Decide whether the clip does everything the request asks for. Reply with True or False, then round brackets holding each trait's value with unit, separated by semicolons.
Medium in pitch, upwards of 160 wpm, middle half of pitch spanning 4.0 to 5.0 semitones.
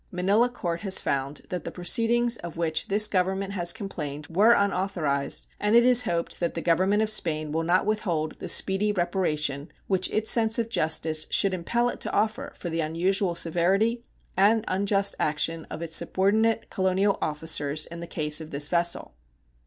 True (180 Hz; 175 wpm; 4.3 semitones)